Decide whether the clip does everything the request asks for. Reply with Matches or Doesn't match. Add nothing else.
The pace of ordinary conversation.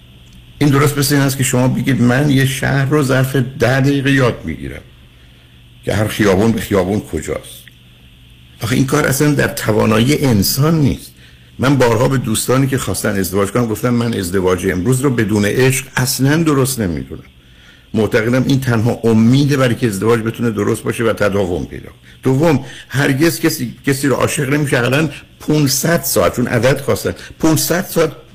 Doesn't match